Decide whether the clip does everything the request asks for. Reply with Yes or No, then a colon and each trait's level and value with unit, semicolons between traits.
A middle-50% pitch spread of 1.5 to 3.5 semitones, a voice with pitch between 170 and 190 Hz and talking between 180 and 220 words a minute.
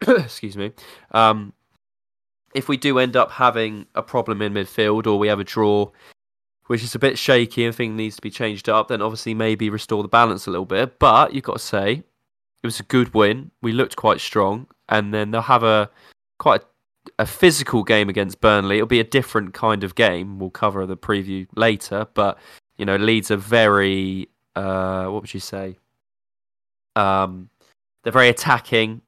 No: average, 2.7 semitones; low, 110 Hz; average, 190 wpm